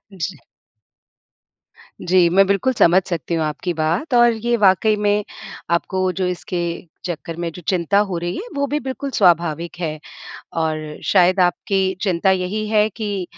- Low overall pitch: No, medium, 185 Hz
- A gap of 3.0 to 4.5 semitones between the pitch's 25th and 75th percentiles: Yes, average, 3.4 semitones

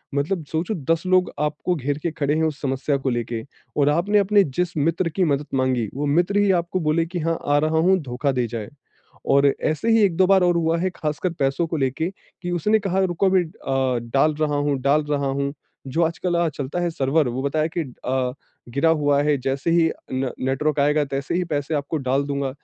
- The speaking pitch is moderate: Yes, medium, 150 Hz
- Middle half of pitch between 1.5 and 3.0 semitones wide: No, average, 3.7 semitones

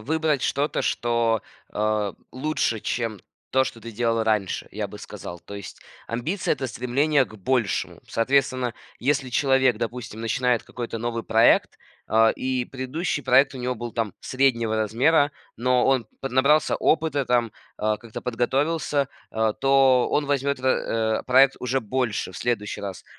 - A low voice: Yes, low, 125 Hz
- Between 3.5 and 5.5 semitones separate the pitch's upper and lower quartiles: No, average, 3.1 semitones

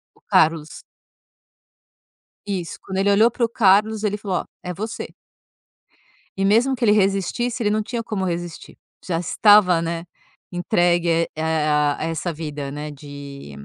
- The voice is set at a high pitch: No, medium, 180 Hz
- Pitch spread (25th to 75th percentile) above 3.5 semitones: Yes, average, 4.5 semitones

